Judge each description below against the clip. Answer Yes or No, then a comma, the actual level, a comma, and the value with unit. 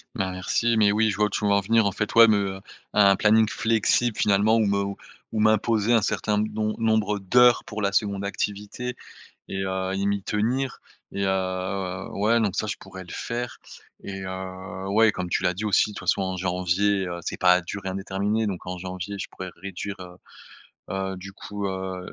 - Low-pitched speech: Yes, low, 100 Hz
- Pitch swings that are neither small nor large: No, narrow, 2.3 semitones